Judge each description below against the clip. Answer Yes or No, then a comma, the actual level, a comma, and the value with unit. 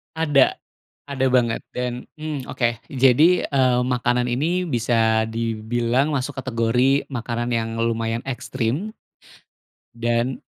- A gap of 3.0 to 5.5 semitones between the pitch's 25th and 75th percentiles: No, narrow, 2.5 semitones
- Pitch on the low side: Yes, low, 125 Hz